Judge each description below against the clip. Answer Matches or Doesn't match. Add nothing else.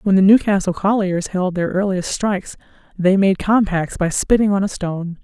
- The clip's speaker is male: Doesn't match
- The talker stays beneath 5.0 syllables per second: Doesn't match